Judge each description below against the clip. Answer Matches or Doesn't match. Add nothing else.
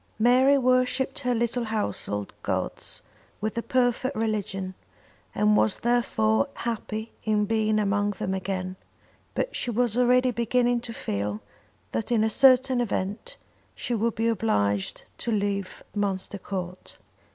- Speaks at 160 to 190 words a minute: Doesn't match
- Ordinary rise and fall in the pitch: Matches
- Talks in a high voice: Matches